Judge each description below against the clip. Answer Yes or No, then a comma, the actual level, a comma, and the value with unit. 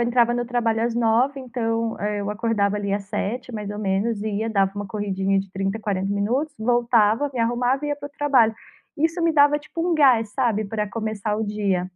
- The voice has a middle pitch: No, high, 225 Hz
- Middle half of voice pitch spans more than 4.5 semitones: No, average, 3.2 semitones